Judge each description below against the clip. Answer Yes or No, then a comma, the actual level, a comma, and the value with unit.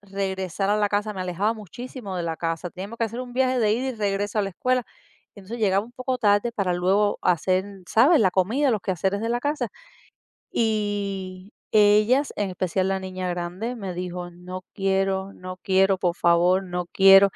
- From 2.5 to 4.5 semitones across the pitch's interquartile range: Yes, average, 2.9 semitones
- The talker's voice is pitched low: No, high, 195 Hz